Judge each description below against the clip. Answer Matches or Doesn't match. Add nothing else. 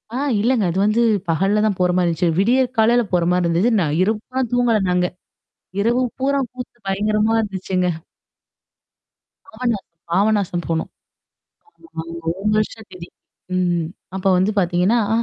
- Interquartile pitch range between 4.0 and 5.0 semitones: Matches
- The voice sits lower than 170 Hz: Doesn't match